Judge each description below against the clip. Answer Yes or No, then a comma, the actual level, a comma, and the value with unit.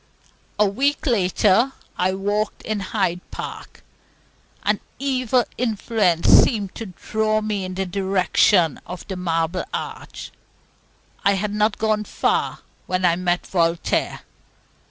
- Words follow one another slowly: Yes, slow, 125 wpm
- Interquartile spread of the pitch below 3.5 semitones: Yes, average, 3.0 semitones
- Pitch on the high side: Yes, high, 200 Hz